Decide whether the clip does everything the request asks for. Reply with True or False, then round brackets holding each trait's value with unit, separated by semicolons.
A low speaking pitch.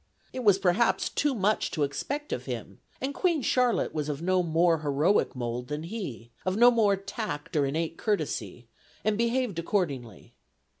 False (185 Hz)